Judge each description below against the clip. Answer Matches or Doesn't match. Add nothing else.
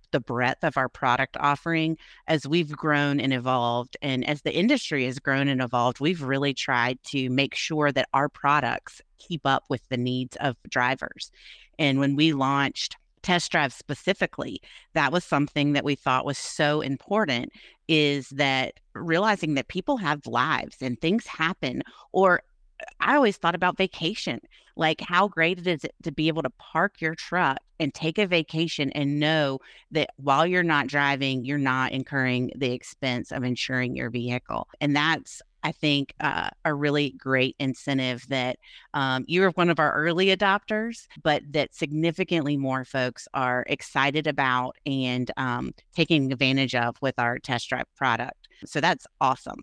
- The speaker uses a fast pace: Doesn't match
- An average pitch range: Matches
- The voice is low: Doesn't match